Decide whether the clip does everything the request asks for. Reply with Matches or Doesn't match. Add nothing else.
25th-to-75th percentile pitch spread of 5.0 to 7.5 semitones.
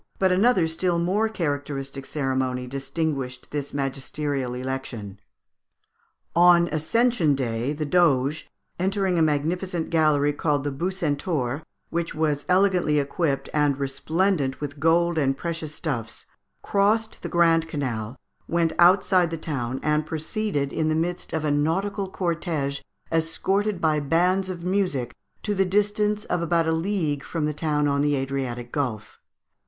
Doesn't match